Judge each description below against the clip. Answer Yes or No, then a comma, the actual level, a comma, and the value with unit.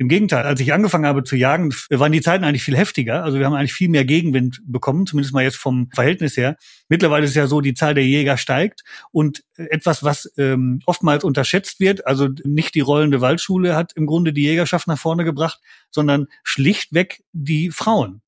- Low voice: No, medium, 150 Hz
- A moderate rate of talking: No, fast, 200 wpm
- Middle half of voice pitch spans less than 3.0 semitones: No, average, 3.4 semitones